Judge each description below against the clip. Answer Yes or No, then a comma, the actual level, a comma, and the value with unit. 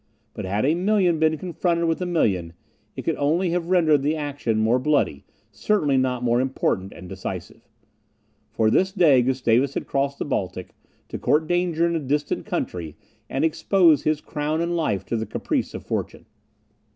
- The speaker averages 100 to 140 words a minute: No, average, 175 wpm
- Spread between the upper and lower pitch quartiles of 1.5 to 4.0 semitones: No, wide, 5.4 semitones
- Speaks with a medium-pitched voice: Yes, medium, 145 Hz